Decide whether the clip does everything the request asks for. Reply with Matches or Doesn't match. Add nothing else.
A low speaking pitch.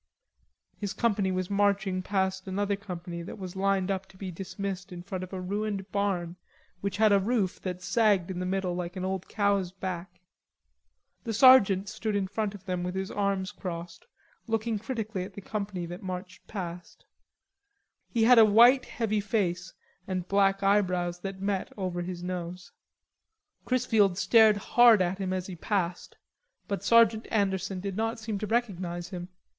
Doesn't match